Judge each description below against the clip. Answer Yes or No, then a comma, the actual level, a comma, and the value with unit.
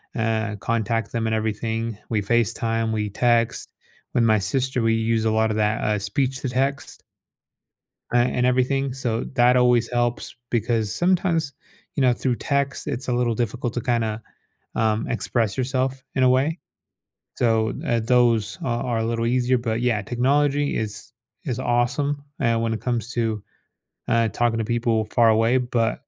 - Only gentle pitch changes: Yes, narrow, 2.1 semitones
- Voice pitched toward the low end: Yes, low, 120 Hz